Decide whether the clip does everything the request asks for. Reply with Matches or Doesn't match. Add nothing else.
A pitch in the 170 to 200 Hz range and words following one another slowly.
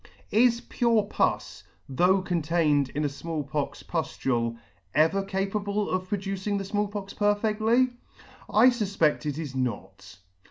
Matches